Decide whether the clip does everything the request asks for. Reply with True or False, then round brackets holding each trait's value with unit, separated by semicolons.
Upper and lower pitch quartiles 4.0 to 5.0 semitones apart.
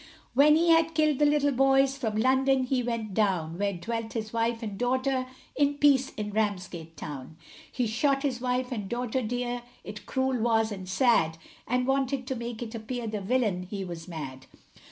True (4.3 semitones)